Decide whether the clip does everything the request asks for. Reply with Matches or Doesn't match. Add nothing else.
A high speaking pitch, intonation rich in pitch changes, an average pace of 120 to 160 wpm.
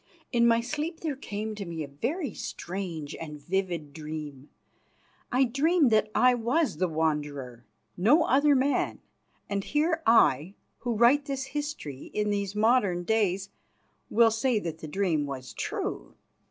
Matches